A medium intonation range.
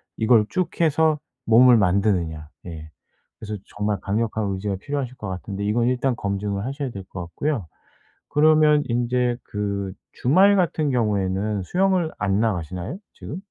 No: wide, 6.1 semitones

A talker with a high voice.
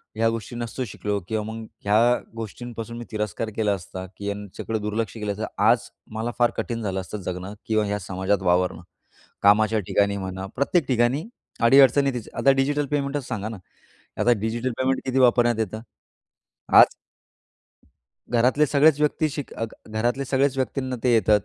No: low, 115 Hz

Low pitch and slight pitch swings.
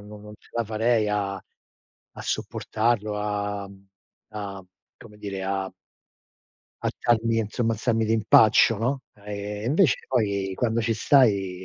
Yes: low, 105 Hz; narrow, 2.1 semitones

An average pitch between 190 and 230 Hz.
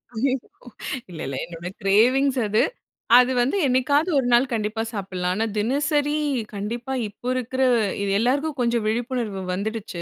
No: high, 240 Hz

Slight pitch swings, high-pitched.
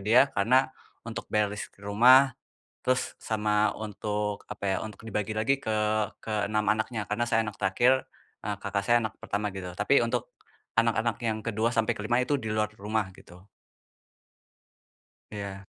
No: narrow, 2.0 semitones; low, 110 Hz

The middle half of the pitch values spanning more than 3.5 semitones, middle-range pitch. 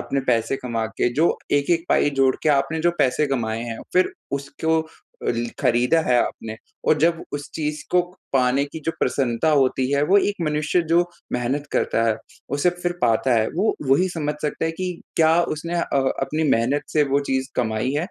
Yes: average, 4.4 semitones; medium, 145 Hz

